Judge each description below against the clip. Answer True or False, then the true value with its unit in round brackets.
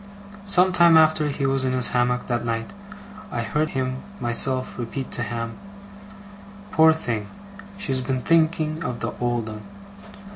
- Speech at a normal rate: True (150 wpm)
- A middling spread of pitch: True (4.6 semitones)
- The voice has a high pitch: False (130 Hz)